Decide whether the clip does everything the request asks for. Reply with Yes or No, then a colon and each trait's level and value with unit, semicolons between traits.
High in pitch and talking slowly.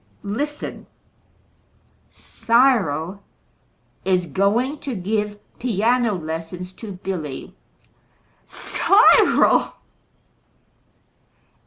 Yes: high, 200 Hz; slow, 55 wpm